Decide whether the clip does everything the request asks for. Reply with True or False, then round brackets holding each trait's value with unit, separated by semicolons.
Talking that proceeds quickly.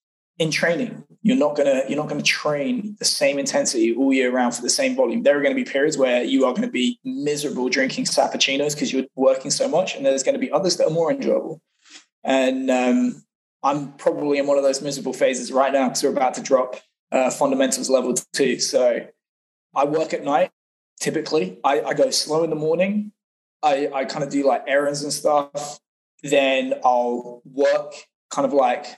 False (195 wpm)